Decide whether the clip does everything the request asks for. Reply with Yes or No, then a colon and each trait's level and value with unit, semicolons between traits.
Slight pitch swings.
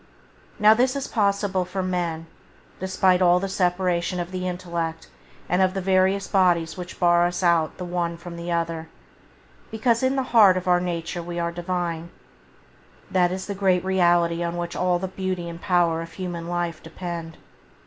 Yes: narrow, 1.7 semitones